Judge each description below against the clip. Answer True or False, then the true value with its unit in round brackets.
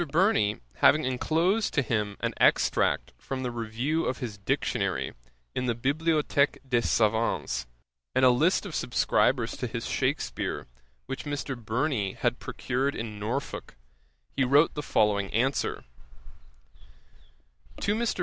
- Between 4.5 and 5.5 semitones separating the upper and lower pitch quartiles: True (5.0 semitones)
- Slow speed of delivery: True (130 wpm)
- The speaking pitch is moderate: False (130 Hz)